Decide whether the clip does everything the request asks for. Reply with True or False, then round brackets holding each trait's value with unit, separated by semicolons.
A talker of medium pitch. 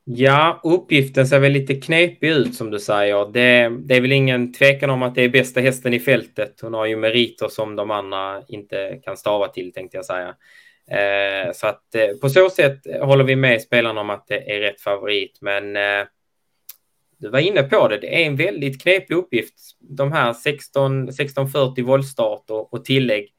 False (125 Hz)